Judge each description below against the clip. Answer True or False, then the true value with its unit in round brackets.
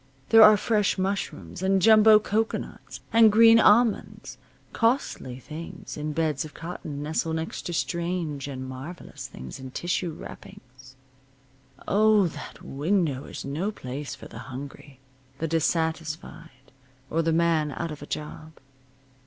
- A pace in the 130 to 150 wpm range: True (135 wpm)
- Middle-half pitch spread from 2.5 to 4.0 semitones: False (5.5 semitones)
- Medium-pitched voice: True (160 Hz)